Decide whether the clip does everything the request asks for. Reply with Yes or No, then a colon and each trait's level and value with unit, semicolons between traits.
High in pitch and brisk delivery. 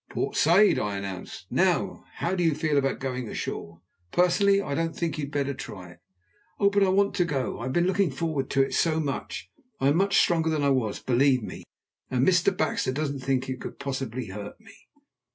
No: medium, 140 Hz; fast, 215 wpm